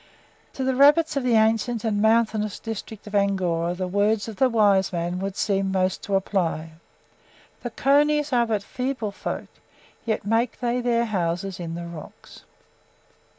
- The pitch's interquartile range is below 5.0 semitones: Yes, average, 3.8 semitones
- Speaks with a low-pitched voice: No, high, 210 Hz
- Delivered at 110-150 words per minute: No, average, 160 wpm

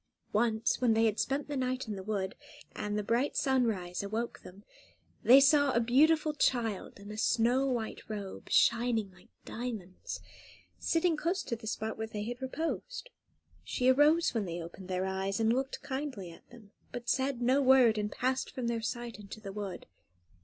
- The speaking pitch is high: Yes, high, 235 Hz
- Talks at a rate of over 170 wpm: Yes, average, 180 wpm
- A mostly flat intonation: No, average, 4.1 semitones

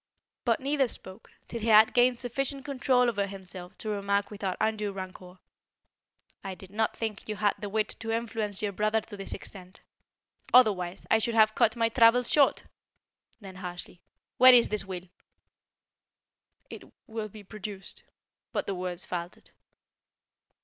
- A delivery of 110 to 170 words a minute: Yes, average, 155 wpm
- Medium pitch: No, high, 210 Hz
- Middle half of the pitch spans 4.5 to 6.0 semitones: No, average, 3.1 semitones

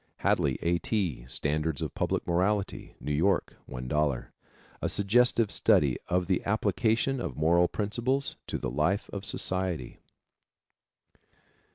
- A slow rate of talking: Yes, slow, 125 wpm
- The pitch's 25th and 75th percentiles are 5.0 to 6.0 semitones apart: Yes, wide, 5.6 semitones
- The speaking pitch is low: Yes, very low, 90 Hz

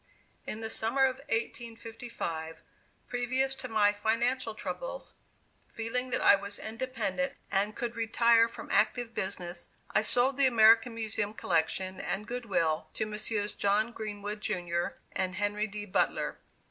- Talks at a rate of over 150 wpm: No, average, 140 wpm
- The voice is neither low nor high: No, high, 220 Hz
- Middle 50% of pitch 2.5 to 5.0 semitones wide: Yes, average, 2.9 semitones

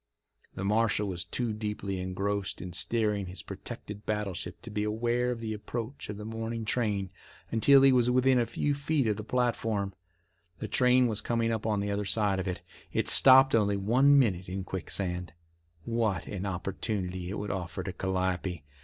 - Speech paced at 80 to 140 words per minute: No, average, 180 wpm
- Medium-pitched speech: No, low, 105 Hz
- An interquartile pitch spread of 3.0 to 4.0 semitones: Yes, average, 3.4 semitones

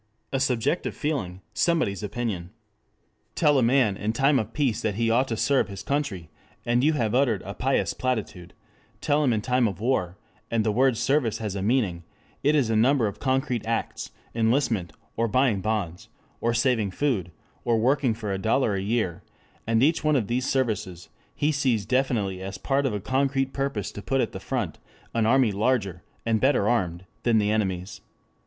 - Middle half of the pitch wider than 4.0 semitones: Yes, average, 4.6 semitones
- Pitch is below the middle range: Yes, low, 115 Hz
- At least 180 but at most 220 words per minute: Yes, average, 190 wpm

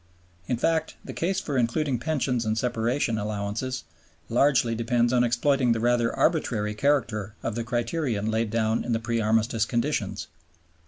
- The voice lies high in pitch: No, low, 120 Hz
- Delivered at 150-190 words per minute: Yes, average, 155 wpm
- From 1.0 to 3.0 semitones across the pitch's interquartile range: Yes, narrow, 2.6 semitones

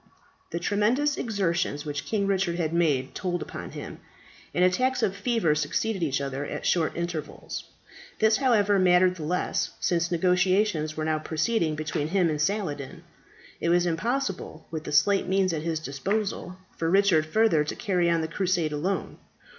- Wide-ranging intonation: No, average, 4.1 semitones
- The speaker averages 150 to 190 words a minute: Yes, average, 165 wpm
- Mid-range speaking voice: Yes, medium, 175 Hz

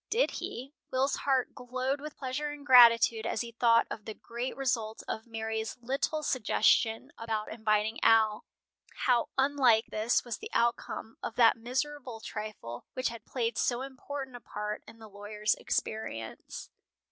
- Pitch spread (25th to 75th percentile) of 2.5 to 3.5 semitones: Yes, average, 2.9 semitones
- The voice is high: Yes, high, 235 Hz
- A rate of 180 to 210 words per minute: No, average, 155 wpm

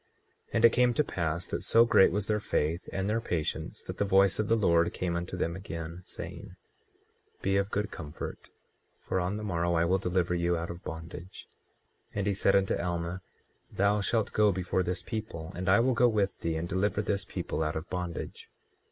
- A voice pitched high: No, very low, 95 Hz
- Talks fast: Yes, fast, 210 wpm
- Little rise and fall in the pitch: No, average, 3.3 semitones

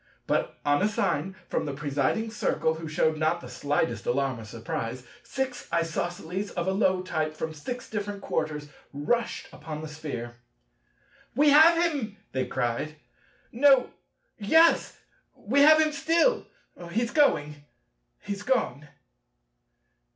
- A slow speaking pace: Yes, slow, 130 wpm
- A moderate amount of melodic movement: No, wide, 8.6 semitones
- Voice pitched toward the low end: No, medium, 175 Hz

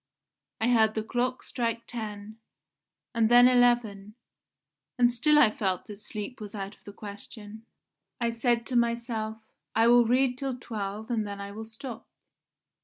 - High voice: Yes, high, 225 Hz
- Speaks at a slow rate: No, average, 160 wpm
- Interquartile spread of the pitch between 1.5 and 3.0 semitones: Yes, narrow, 2.4 semitones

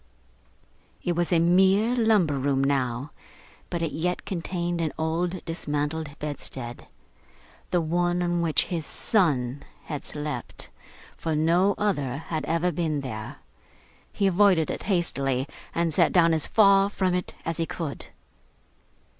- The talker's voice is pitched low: No, medium, 165 Hz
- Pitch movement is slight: No, average, 3.4 semitones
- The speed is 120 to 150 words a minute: Yes, average, 140 wpm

